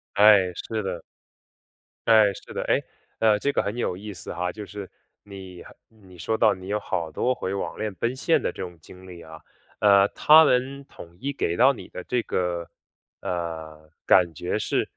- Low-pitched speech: Yes, low, 100 Hz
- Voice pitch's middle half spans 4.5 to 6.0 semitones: No, average, 4.1 semitones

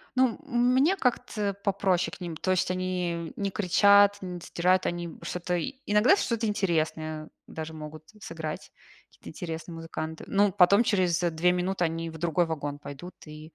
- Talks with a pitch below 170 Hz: No, medium, 180 Hz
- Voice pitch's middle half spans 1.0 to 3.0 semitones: No, average, 3.9 semitones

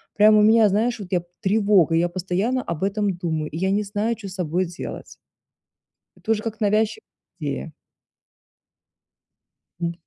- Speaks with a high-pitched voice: Yes, high, 200 Hz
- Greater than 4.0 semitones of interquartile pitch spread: No, average, 3.4 semitones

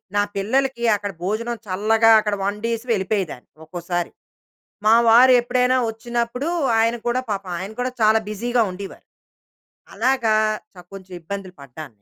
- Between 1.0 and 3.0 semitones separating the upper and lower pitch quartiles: No, average, 3.5 semitones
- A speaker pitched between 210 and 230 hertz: Yes, high, 215 Hz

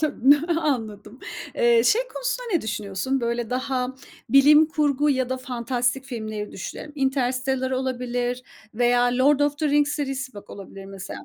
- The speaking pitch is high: Yes, very high, 255 Hz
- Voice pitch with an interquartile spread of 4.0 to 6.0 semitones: No, average, 3.2 semitones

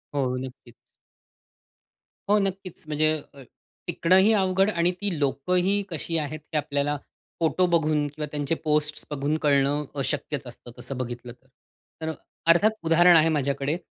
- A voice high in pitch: No, medium, 155 Hz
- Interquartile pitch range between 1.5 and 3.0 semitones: No, average, 3.6 semitones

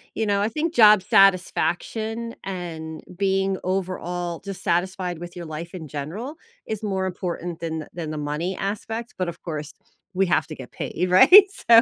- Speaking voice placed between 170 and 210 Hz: Yes, medium, 185 Hz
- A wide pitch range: No, average, 3.0 semitones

